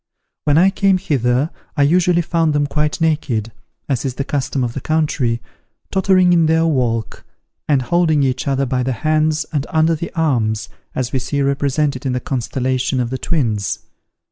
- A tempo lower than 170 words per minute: No, average, 175 wpm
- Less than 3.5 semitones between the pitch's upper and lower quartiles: No, average, 3.9 semitones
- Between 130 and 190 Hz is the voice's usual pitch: Yes, medium, 140 Hz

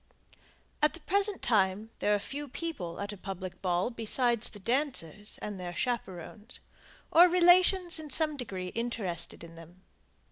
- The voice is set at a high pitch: Yes, high, 225 Hz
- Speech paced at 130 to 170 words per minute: Yes, average, 150 wpm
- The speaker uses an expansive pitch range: Yes, wide, 8.2 semitones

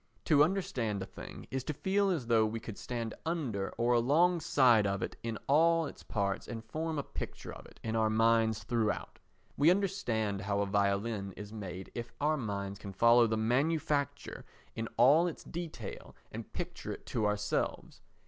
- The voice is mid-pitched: No, low, 115 Hz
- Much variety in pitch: Yes, wide, 6.2 semitones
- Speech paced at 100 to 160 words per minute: No, average, 175 wpm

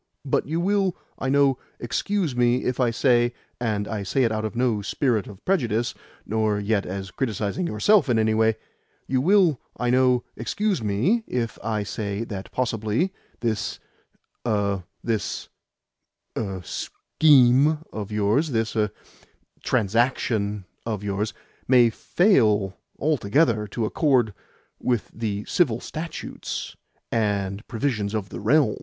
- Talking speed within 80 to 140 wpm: Yes, slow, 135 wpm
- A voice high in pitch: No, low, 115 Hz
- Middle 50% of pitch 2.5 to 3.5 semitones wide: No, average, 4.0 semitones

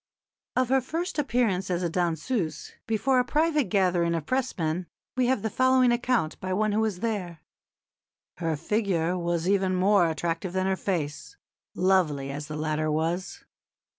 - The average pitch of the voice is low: No, medium, 185 Hz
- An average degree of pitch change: No, wide, 6.1 semitones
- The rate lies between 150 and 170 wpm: Yes, average, 160 wpm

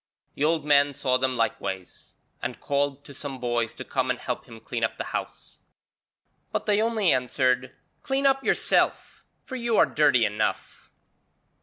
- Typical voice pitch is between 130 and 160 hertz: Yes, low, 135 Hz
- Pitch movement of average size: Yes, average, 3.8 semitones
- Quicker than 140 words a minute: Yes, average, 165 wpm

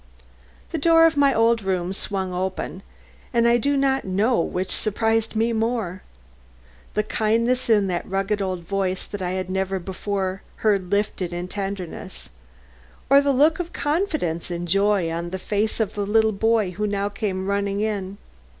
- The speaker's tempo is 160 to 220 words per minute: Yes, average, 165 wpm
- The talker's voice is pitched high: Yes, high, 200 Hz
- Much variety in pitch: No, average, 3.2 semitones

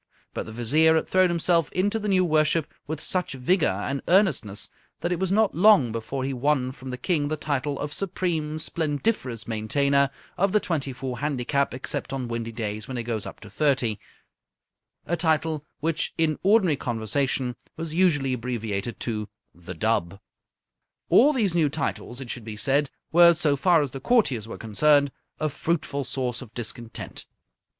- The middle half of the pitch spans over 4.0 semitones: Yes, average, 5.3 semitones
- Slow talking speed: No, average, 175 wpm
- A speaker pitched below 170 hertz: Yes, medium, 140 Hz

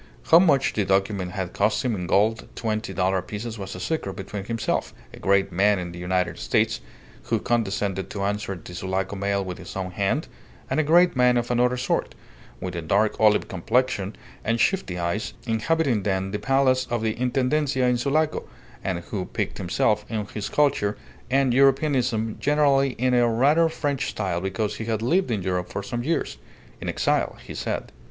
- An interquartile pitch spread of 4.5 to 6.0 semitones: Yes, average, 4.9 semitones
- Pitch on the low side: Yes, low, 110 Hz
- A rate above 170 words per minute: Yes, average, 185 wpm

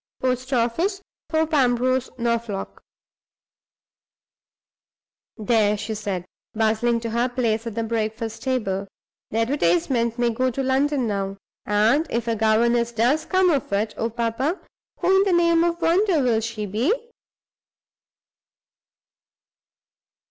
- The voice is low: No, high, 235 Hz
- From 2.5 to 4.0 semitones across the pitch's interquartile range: Yes, average, 3.5 semitones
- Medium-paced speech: No, slow, 125 wpm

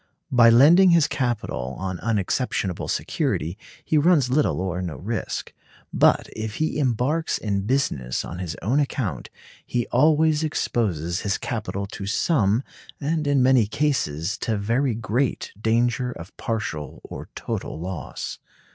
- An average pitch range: No, wide, 6.5 semitones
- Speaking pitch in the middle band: No, low, 115 Hz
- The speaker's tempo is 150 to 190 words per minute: No, average, 140 wpm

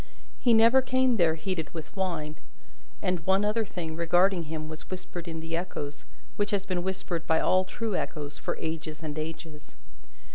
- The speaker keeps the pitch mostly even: No, average, 3.3 semitones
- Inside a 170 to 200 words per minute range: Yes, average, 175 wpm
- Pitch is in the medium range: Yes, medium, 175 Hz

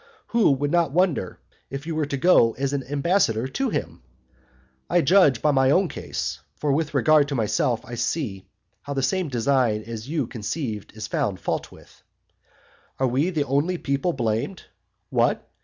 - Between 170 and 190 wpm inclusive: Yes, average, 175 wpm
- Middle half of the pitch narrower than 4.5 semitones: No, average, 5.1 semitones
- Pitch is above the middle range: No, medium, 140 Hz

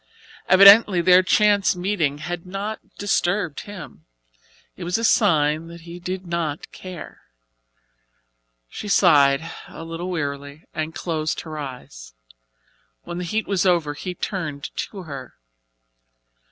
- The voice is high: No, medium, 170 Hz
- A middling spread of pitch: Yes, average, 3.7 semitones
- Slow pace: Yes, slow, 125 wpm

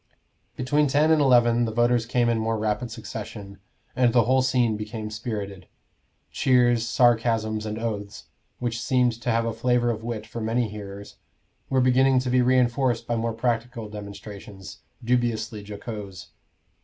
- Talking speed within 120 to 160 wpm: Yes, average, 155 wpm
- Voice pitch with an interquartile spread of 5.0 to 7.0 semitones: No, narrow, 2.4 semitones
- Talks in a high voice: No, low, 115 Hz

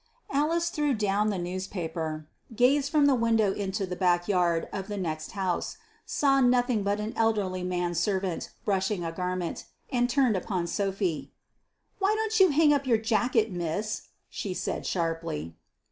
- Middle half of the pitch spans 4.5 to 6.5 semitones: Yes, wide, 5.5 semitones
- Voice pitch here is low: No, high, 200 Hz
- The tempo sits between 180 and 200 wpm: No, average, 160 wpm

